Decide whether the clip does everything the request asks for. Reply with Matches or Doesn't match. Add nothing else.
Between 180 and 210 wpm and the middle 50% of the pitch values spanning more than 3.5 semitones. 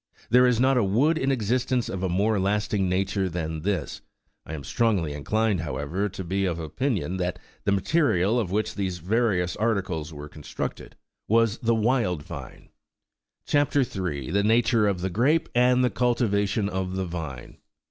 Doesn't match